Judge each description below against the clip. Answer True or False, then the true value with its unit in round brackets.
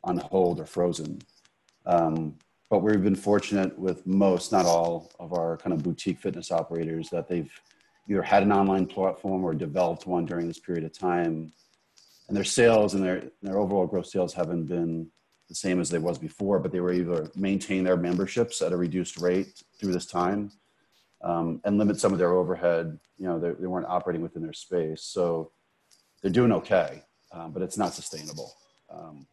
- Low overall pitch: True (90 Hz)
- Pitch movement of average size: False (2.3 semitones)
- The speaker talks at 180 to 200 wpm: True (190 wpm)